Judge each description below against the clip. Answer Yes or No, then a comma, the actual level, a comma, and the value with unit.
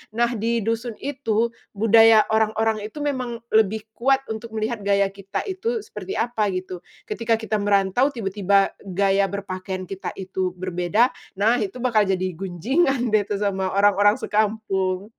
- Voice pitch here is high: Yes, high, 215 Hz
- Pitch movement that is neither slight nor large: Yes, average, 3.0 semitones